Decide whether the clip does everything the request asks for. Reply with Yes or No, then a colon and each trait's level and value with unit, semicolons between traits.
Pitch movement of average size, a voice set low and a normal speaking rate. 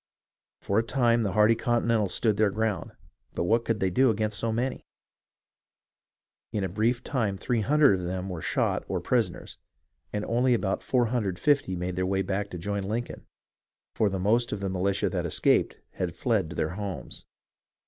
Yes: average, 3.5 semitones; low, 105 Hz; average, 175 wpm